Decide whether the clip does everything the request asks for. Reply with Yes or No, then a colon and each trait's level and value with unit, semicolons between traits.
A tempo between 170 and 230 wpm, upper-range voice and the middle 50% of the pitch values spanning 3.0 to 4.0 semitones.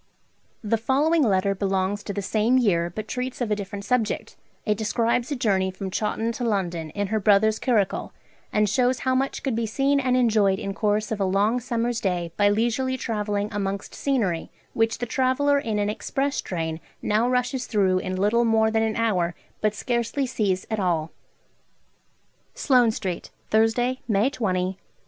Yes: average, 175 wpm; high, 220 Hz; average, 3.6 semitones